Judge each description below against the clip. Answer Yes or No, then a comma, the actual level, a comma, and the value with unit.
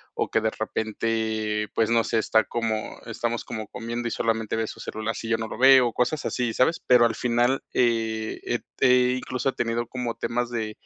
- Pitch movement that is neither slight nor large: No, narrow, 1.6 semitones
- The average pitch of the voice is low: Yes, low, 115 Hz